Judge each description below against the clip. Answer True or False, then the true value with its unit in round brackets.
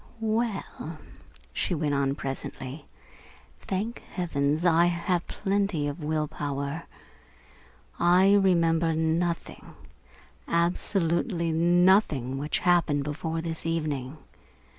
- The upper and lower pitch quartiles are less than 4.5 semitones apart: True (3.1 semitones)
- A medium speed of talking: False (95 wpm)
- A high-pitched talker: False (165 Hz)